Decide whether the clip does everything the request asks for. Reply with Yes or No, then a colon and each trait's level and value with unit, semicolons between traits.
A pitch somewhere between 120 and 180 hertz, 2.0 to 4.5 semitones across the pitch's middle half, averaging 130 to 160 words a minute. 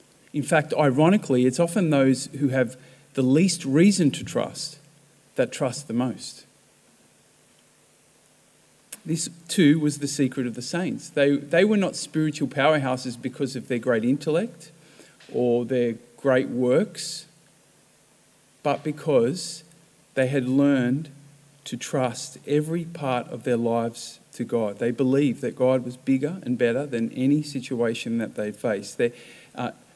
Yes: medium, 140 Hz; average, 3.5 semitones; average, 140 wpm